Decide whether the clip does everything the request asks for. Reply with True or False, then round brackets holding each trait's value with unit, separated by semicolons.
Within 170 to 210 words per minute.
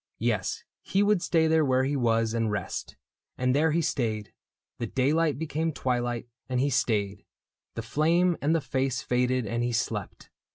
True (175 wpm)